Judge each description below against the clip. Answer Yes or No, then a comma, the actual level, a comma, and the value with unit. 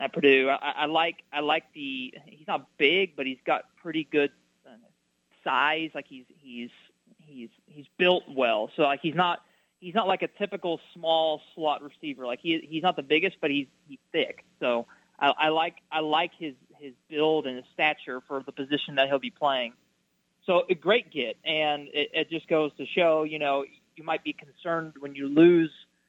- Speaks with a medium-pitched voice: Yes, medium, 155 Hz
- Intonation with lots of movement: No, average, 3.2 semitones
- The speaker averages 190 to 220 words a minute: Yes, average, 200 wpm